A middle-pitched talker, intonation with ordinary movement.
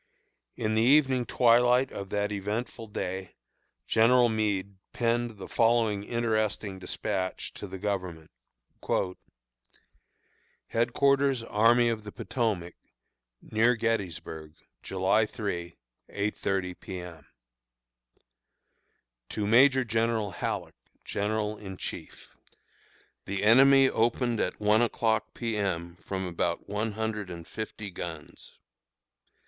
No: low, 110 Hz; average, 3.4 semitones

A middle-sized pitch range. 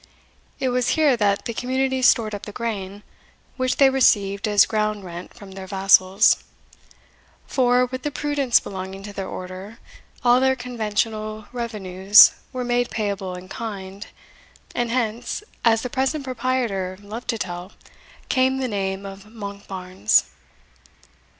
Yes: average, 4.3 semitones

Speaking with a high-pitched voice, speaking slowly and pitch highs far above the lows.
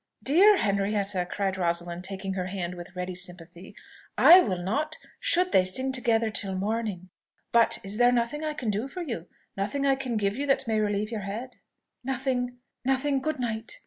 No: high, 220 Hz; average, 180 wpm; wide, 5.7 semitones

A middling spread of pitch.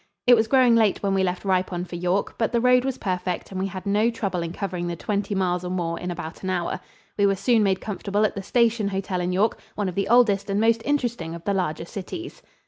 Yes: average, 3.5 semitones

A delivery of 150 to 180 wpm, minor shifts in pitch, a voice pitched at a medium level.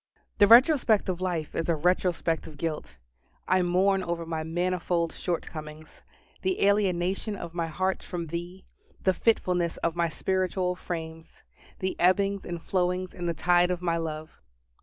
Yes: average, 155 wpm; narrow, 2.1 semitones; medium, 175 Hz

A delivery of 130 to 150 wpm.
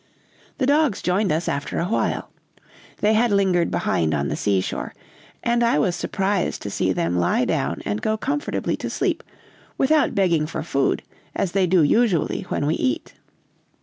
No: average, 170 wpm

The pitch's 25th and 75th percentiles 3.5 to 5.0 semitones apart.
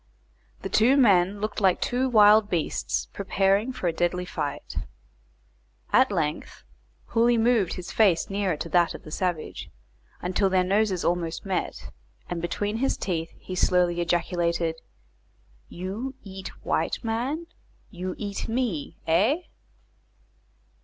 Yes: average, 4.1 semitones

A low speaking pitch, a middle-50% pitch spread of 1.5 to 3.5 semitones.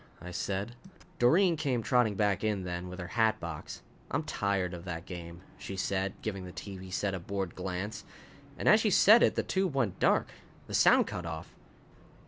No: very low, 95 Hz; average, 3.9 semitones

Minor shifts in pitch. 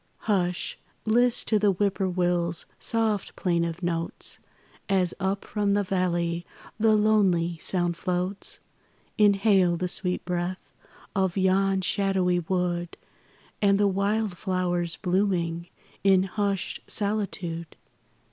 Yes: narrow, 2.3 semitones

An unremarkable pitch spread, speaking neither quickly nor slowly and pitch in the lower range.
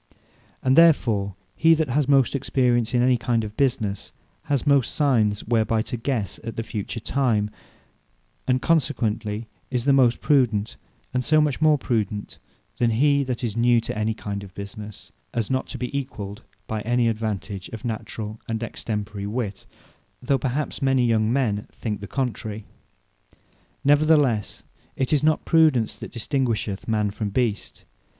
Yes: average, 3.9 semitones; average, 155 wpm; low, 115 Hz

